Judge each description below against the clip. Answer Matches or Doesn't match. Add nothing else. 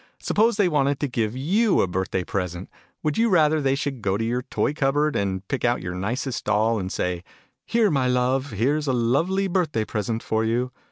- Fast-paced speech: Matches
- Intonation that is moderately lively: Doesn't match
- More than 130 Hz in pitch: Doesn't match